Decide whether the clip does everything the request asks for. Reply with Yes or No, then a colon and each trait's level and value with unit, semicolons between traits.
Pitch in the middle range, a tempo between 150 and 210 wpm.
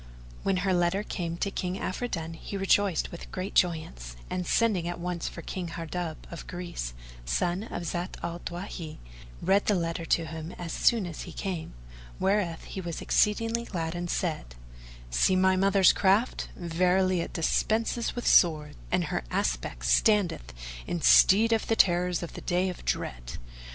Yes: medium, 175 Hz; average, 160 wpm